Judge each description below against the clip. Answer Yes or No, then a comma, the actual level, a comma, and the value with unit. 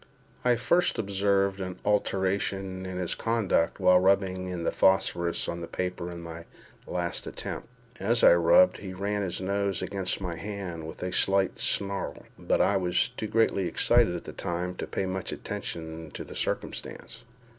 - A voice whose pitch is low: Yes, very low, 95 Hz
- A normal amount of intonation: No, narrow, 2.0 semitones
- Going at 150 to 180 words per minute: Yes, average, 170 wpm